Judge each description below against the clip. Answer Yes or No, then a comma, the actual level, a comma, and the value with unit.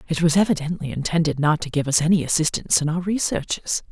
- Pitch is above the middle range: No, medium, 165 Hz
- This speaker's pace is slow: No, average, 200 wpm